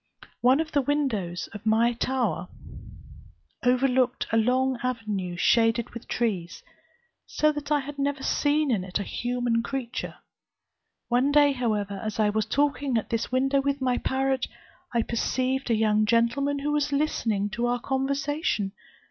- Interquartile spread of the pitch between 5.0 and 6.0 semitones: No, average, 3.8 semitones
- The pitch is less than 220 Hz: No, very high, 250 Hz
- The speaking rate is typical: Yes, average, 155 wpm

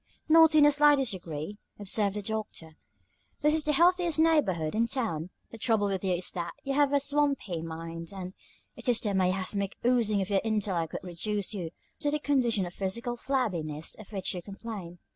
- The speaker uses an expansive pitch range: Yes, wide, 7.0 semitones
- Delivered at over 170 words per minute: Yes, average, 190 wpm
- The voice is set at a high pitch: Yes, high, 210 Hz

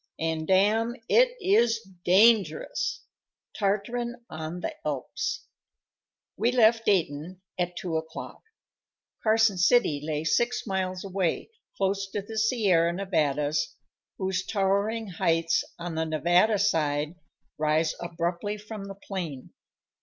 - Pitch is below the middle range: No, high, 190 Hz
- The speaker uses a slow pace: Yes, slow, 115 wpm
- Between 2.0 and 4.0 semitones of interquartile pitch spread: No, average, 5.0 semitones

